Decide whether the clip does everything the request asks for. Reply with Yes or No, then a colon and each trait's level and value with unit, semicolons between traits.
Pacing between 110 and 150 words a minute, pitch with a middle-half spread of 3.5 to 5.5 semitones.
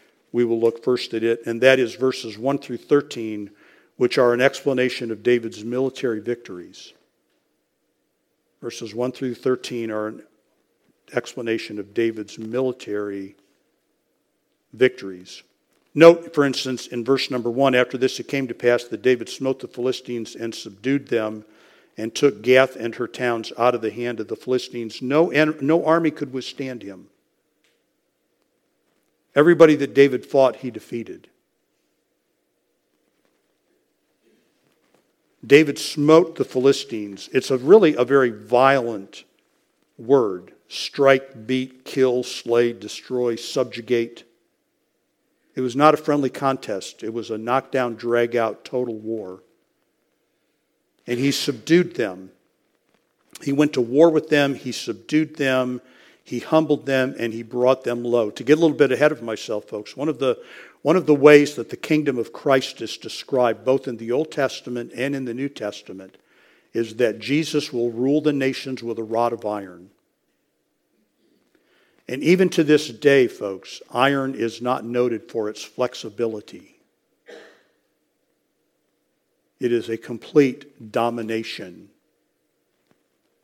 No: average, 140 wpm; average, 3.1 semitones